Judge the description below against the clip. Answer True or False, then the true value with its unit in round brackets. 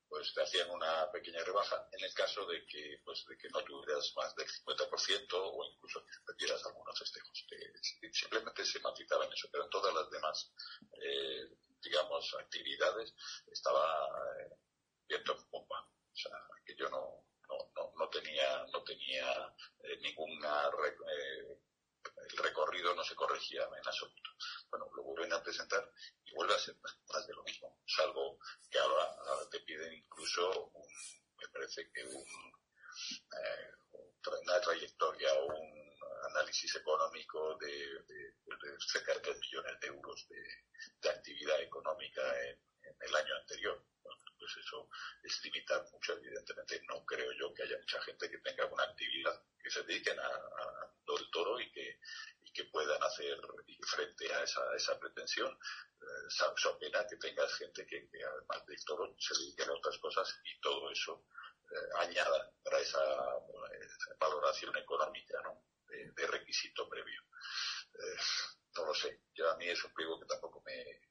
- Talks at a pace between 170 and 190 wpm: False (160 wpm)